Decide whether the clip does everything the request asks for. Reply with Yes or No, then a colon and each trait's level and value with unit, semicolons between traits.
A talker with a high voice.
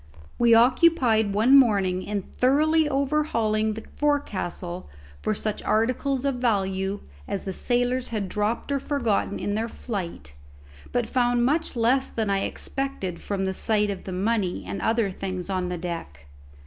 Yes: high, 220 Hz